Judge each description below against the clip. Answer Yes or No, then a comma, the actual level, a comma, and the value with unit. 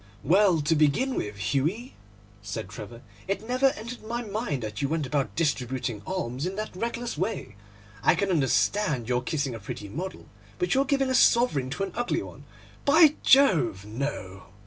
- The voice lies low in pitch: No, medium, 165 Hz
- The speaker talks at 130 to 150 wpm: No, average, 170 wpm